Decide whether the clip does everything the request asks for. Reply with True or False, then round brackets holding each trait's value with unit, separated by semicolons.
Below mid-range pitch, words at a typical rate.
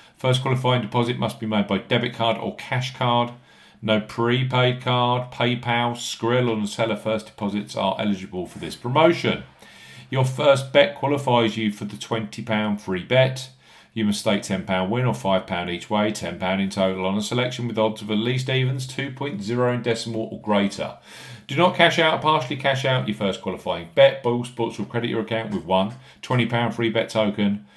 True (115 Hz; 185 wpm)